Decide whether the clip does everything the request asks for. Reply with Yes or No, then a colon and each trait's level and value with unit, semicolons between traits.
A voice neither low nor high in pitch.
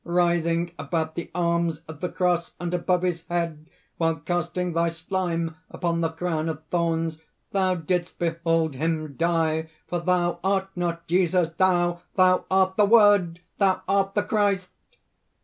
Yes: medium, 170 Hz